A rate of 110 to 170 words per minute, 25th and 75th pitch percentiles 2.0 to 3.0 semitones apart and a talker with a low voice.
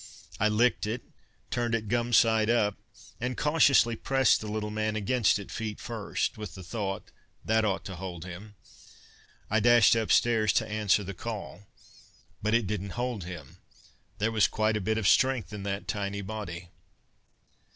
Yes: average, 165 wpm; narrow, 2.6 semitones; low, 110 Hz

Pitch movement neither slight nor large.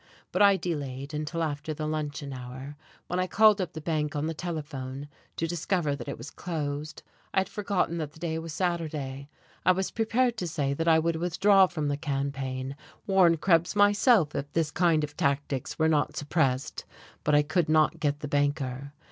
Yes: average, 3.4 semitones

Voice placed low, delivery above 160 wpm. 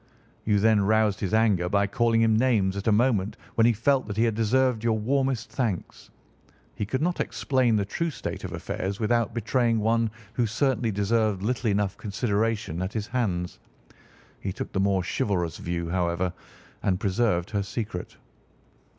Yes: low, 110 Hz; average, 170 wpm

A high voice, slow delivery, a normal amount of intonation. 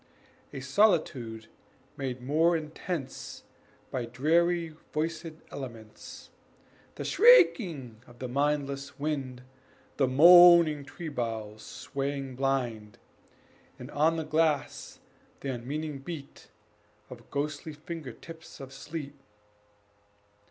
No: medium, 140 Hz; slow, 100 wpm; average, 3.9 semitones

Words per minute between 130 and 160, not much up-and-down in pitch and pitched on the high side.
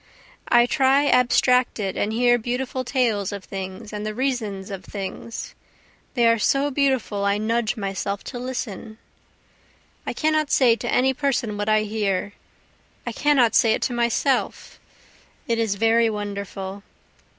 No: average, 145 wpm; average, 3.6 semitones; high, 230 Hz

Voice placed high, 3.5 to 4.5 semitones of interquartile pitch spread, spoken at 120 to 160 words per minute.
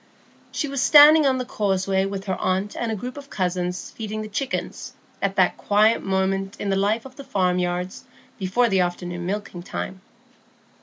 No: high, 195 Hz; average, 3.8 semitones; average, 175 wpm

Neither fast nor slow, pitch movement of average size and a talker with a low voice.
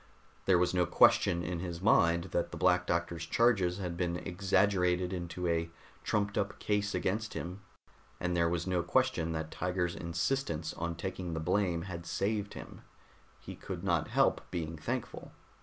No: average, 165 wpm; narrow, 2.1 semitones; very low, 90 Hz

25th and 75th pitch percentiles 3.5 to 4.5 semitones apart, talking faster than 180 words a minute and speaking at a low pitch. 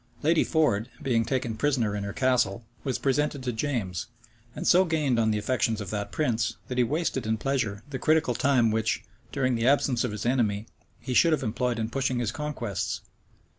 Yes: average, 3.9 semitones; average, 195 wpm; low, 125 Hz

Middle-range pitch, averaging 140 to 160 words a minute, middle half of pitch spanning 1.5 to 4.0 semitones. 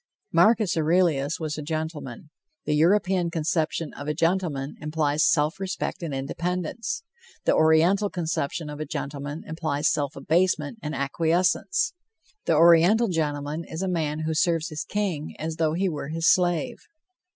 Yes: medium, 160 Hz; average, 150 wpm; average, 2.9 semitones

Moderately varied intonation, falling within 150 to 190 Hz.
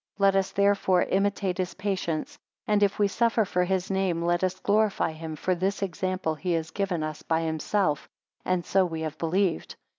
Yes: average, 3.0 semitones; medium, 185 Hz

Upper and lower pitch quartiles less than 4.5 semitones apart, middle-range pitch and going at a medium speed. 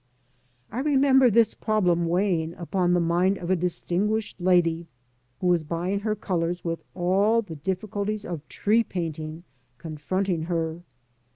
Yes: average, 3.4 semitones; medium, 180 Hz; average, 145 wpm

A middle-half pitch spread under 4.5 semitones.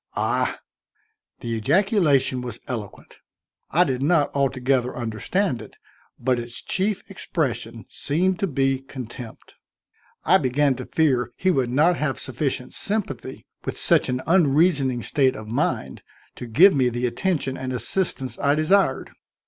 No: average, 4.9 semitones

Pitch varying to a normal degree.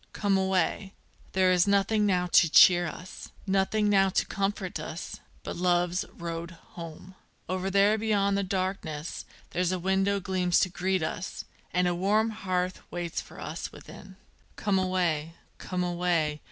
No: narrow, 1.9 semitones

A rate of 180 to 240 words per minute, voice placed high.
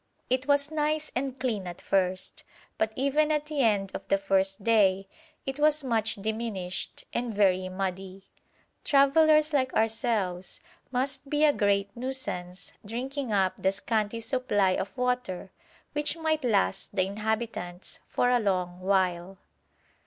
No: average, 140 wpm; high, 220 Hz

